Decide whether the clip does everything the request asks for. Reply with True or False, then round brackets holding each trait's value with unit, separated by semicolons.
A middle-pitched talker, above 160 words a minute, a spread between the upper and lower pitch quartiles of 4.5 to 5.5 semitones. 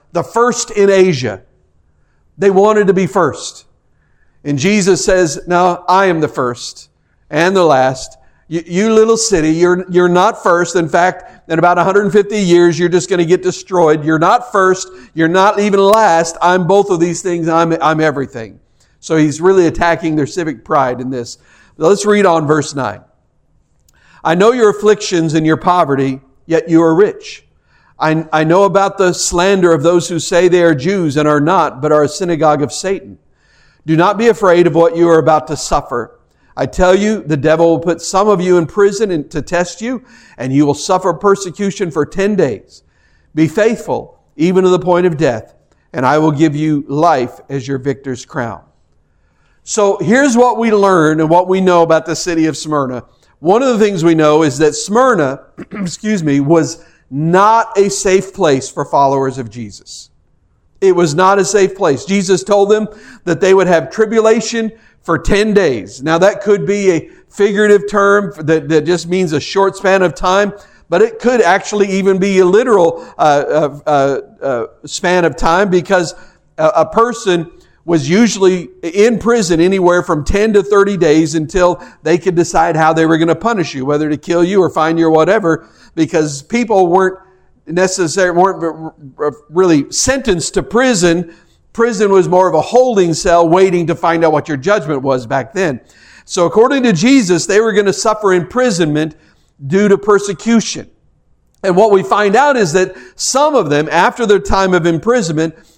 False (175 Hz; 185 wpm; 4.0 semitones)